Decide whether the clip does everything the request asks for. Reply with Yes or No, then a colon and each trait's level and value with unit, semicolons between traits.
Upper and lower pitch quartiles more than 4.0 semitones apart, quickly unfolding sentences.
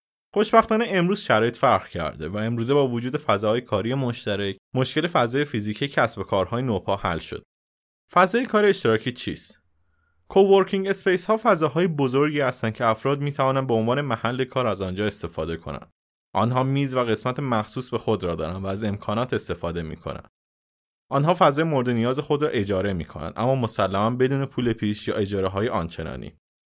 Yes: wide, 5.5 semitones; fast, 170 wpm